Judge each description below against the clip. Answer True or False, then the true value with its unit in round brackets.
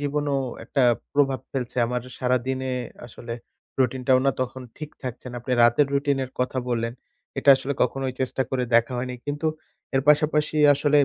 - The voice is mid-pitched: False (130 Hz)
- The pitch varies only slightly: True (2.2 semitones)